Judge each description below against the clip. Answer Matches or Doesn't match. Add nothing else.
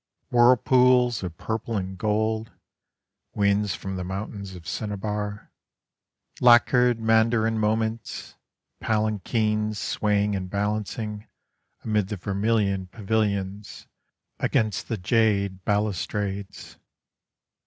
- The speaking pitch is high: Doesn't match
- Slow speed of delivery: Matches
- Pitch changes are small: Matches